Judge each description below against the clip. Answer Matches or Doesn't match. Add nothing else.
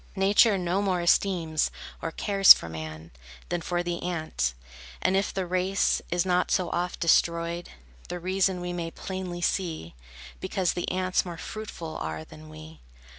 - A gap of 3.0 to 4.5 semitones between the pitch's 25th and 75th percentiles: Doesn't match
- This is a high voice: Doesn't match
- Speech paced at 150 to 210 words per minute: Matches